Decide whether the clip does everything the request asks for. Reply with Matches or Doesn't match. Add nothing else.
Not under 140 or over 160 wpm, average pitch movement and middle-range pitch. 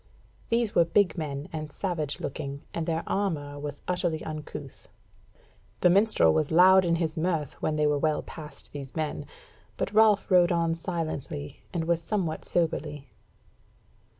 Matches